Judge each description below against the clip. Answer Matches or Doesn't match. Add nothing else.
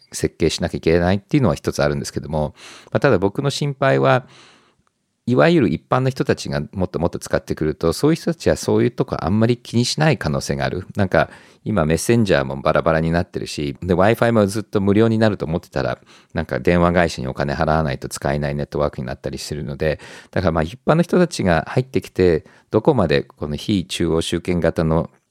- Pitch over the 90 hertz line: Doesn't match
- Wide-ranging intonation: Matches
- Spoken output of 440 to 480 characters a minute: Matches